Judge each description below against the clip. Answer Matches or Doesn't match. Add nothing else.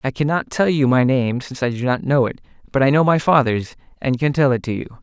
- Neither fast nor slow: Doesn't match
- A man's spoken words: Matches